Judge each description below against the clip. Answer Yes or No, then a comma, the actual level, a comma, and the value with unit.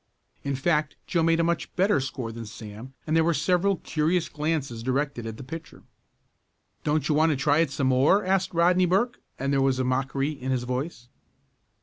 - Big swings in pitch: No, average, 4.2 semitones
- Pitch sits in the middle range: Yes, medium, 150 Hz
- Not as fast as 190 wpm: No, average, 195 wpm